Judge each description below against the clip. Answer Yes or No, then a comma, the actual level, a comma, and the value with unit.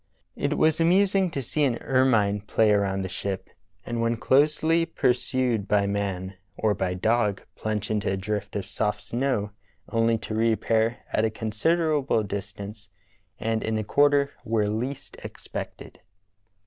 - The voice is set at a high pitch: No, low, 110 Hz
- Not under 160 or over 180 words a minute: No, average, 150 wpm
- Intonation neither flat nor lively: Yes, average, 4.3 semitones